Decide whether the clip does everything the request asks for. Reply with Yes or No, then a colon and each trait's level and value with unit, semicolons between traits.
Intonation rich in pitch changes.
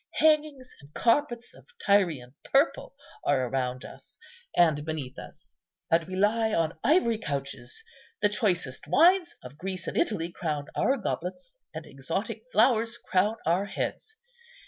Yes: wide, 7.7 semitones